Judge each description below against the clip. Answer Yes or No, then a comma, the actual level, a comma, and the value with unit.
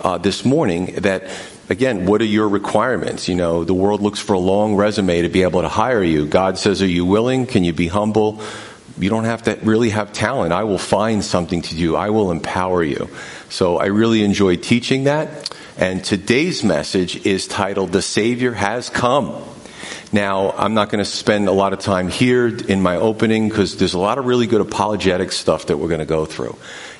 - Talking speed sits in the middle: No, fast, 210 wpm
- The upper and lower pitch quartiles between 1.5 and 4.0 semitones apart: Yes, average, 3.0 semitones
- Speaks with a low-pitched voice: Yes, low, 100 Hz